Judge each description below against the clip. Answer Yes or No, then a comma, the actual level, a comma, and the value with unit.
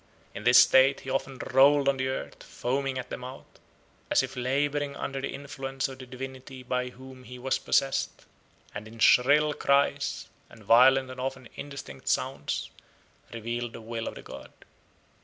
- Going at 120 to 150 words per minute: No, average, 170 wpm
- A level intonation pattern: Yes, narrow, 1.6 semitones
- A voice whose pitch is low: Yes, low, 130 Hz